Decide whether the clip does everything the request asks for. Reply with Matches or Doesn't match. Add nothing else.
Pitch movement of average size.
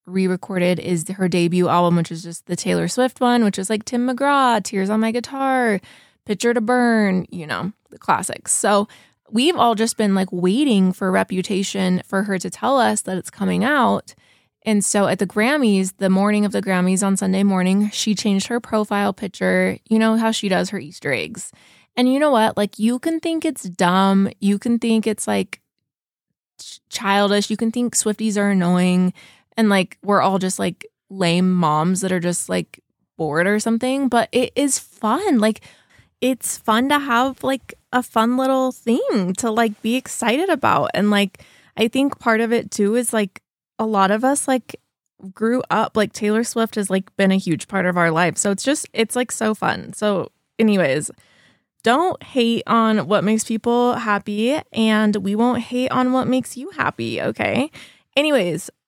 Matches